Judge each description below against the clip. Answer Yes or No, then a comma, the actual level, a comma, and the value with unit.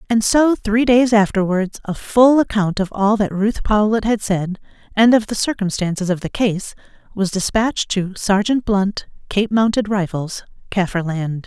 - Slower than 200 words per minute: Yes, average, 160 wpm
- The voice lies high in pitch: Yes, high, 205 Hz